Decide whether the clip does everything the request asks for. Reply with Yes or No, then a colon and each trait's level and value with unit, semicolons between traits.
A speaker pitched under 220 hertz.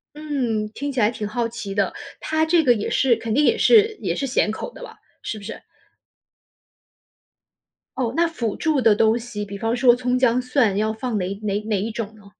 No: high, 235 Hz